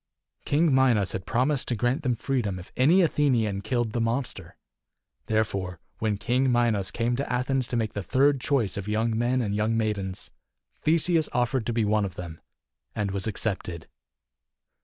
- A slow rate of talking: No, average, 170 wpm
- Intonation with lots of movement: No, average, 3.9 semitones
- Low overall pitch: Yes, low, 115 Hz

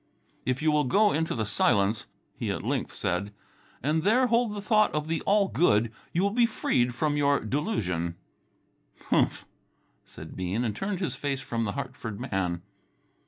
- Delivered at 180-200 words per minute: No, average, 170 wpm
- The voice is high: No, medium, 140 Hz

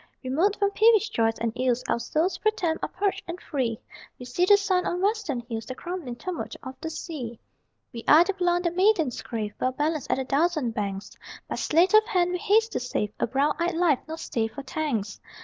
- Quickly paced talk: Yes, fast, 220 wpm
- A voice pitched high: Yes, very high, 315 Hz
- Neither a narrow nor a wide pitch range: No, wide, 6.8 semitones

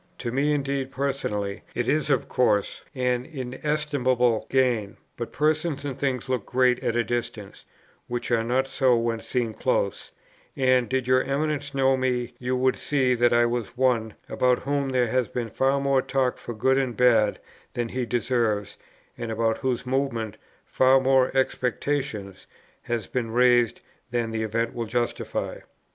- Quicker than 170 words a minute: No, average, 160 wpm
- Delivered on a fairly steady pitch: Yes, narrow, 2.2 semitones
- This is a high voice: No, low, 125 Hz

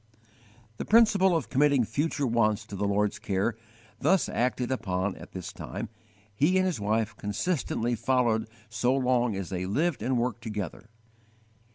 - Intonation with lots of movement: No, average, 4.6 semitones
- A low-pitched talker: Yes, low, 115 Hz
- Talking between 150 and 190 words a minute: Yes, average, 155 wpm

